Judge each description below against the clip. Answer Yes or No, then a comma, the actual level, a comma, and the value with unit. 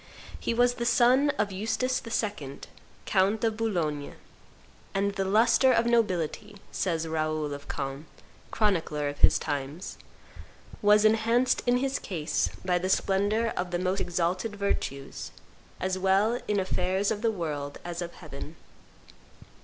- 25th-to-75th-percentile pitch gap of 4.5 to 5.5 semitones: Yes, average, 5.2 semitones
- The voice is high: Yes, high, 195 Hz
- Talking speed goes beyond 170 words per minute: No, average, 140 wpm